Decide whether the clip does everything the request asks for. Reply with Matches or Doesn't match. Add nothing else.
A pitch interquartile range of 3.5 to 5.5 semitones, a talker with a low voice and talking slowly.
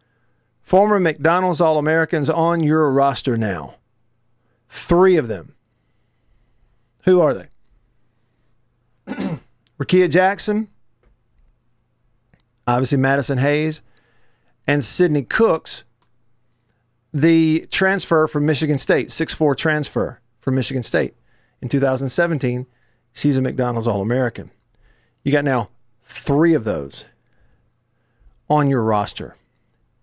Matches